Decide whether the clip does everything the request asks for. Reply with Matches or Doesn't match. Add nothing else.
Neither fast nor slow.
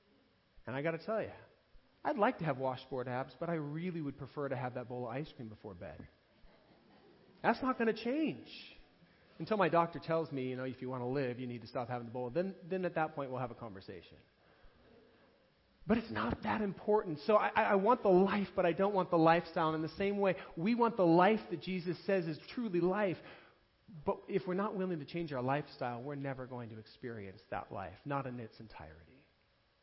Doesn't match